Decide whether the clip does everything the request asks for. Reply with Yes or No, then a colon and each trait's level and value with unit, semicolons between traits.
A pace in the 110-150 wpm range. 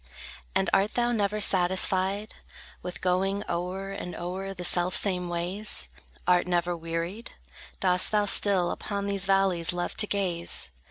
Yes: average, 140 wpm